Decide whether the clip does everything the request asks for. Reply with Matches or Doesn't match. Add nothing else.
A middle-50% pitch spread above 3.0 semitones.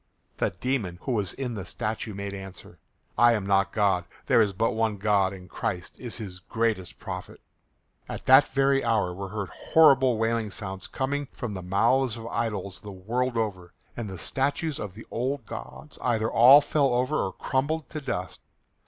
Matches